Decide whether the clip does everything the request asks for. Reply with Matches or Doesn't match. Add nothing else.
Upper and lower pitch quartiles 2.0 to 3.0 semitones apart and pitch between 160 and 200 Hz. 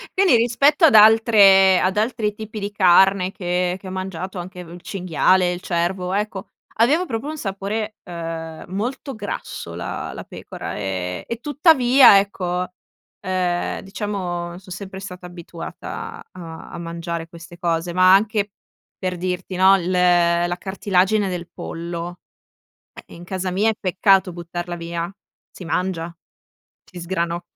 Matches